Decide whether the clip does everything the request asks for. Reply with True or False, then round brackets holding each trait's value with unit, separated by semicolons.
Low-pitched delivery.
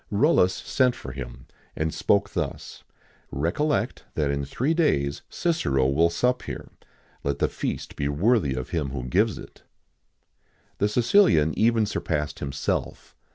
True (85 Hz)